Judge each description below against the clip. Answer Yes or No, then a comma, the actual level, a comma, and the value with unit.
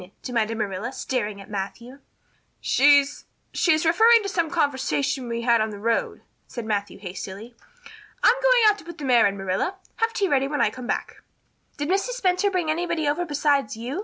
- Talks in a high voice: Yes, very high, 275 Hz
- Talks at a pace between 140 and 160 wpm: No, average, 190 wpm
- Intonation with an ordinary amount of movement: No, wide, 7.2 semitones